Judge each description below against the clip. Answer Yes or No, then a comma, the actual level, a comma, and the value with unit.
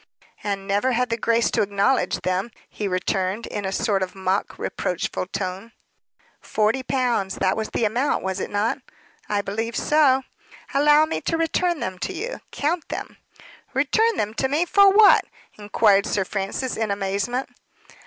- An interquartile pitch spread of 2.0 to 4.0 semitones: No, wide, 5.5 semitones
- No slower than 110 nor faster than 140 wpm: No, average, 165 wpm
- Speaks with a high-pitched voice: Yes, high, 220 Hz